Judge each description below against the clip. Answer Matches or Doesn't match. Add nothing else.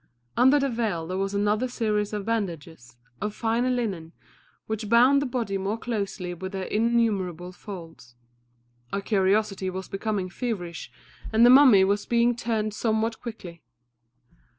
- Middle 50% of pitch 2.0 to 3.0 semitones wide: Doesn't match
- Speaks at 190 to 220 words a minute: Doesn't match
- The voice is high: Matches